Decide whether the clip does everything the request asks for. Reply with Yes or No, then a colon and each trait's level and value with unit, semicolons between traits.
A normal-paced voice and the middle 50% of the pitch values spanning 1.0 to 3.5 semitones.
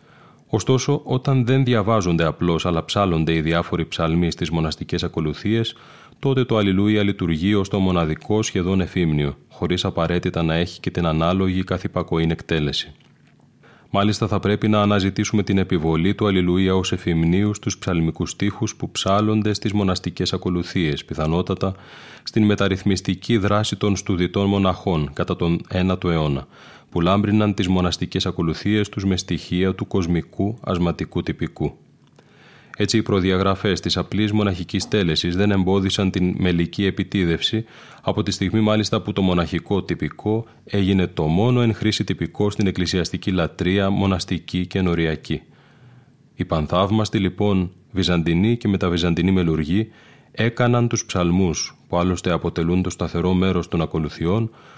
Yes: average, 135 wpm; average, 3.2 semitones